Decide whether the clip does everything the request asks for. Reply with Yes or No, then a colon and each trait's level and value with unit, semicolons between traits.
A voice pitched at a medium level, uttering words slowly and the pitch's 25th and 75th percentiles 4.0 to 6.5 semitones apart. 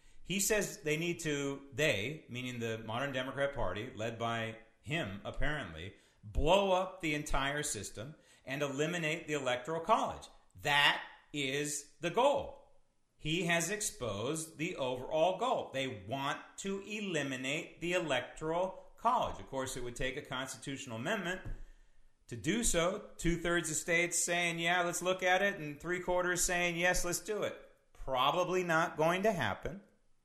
No: medium, 160 Hz; average, 150 wpm; average, 5.1 semitones